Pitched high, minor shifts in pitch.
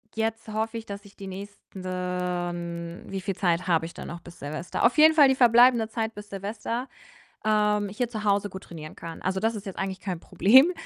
No: high, 200 Hz; average, 3.6 semitones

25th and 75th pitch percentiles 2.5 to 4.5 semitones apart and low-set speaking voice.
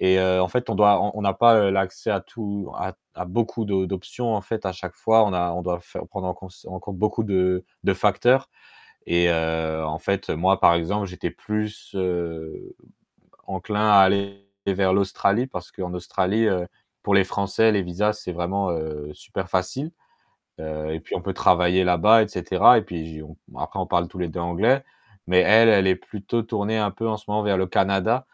Yes: average, 2.9 semitones; very low, 95 Hz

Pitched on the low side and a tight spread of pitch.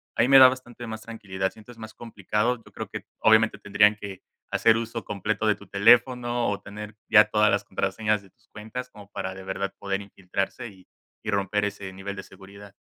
Yes: low, 105 Hz; narrow, 2.3 semitones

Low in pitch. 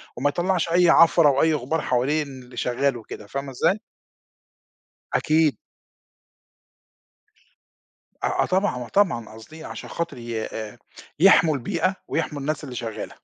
No: medium, 145 Hz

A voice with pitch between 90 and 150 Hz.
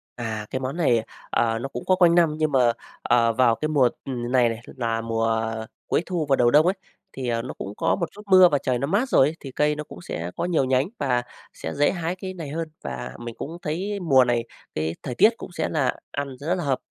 Yes: low, 135 Hz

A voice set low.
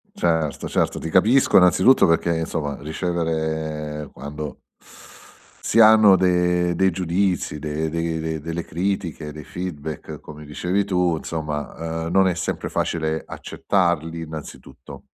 Yes: very low, 80 Hz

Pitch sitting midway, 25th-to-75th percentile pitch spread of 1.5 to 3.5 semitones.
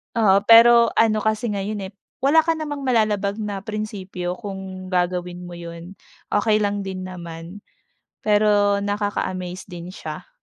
No: high, 205 Hz; average, 2.8 semitones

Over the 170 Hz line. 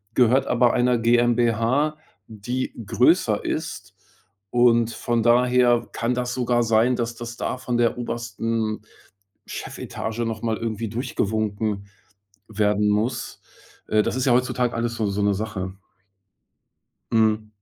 No: low, 115 Hz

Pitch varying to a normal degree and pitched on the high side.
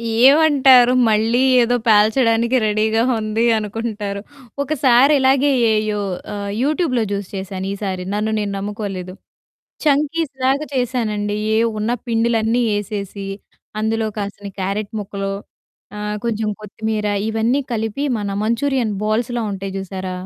Yes: average, 3.1 semitones; high, 220 Hz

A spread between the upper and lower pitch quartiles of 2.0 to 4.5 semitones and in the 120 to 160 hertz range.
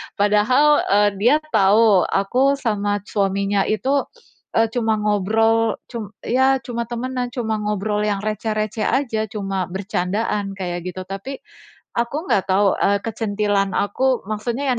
No: average, 2.8 semitones; high, 215 Hz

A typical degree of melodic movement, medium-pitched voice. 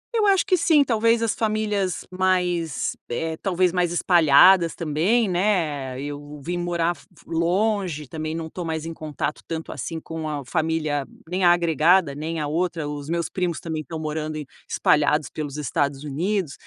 Yes: average, 3.4 semitones; medium, 165 Hz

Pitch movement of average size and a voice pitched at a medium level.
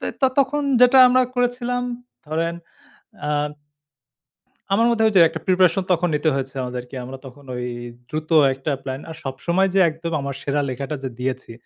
No: wide, 7.2 semitones; medium, 160 Hz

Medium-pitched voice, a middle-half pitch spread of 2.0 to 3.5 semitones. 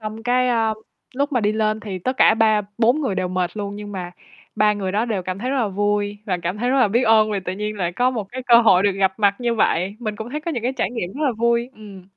No: high, 215 Hz; average, 3.2 semitones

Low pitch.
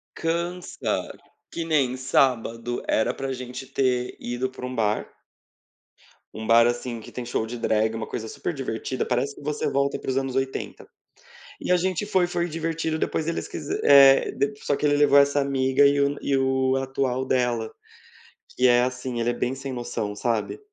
Yes: low, 130 Hz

